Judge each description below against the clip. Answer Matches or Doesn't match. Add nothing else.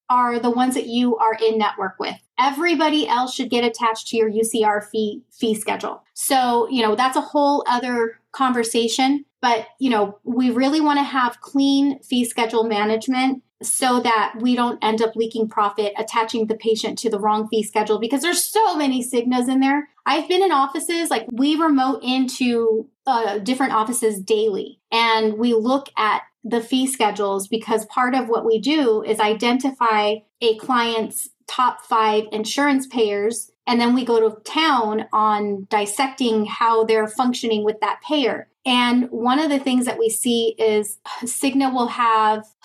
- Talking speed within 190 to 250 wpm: Doesn't match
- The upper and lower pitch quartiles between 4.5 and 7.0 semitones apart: Doesn't match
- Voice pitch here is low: Doesn't match